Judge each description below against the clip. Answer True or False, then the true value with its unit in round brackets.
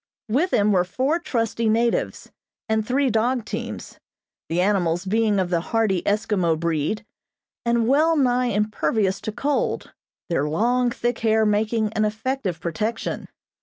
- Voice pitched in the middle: False (220 Hz)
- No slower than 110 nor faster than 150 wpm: True (140 wpm)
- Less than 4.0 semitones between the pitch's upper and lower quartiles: True (3.5 semitones)